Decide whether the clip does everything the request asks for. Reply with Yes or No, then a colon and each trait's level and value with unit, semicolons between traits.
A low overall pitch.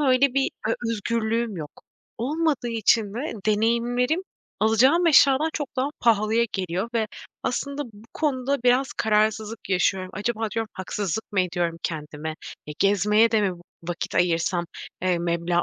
No: high, 220 Hz